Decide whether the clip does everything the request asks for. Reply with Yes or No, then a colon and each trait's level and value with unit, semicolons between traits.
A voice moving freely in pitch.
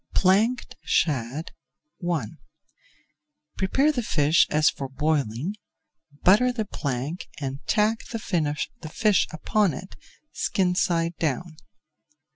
Yes: wide, 5.9 semitones